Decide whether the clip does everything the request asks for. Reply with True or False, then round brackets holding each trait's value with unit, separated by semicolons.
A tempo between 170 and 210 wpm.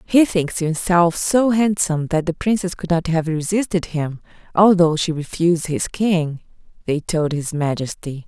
False (160 wpm)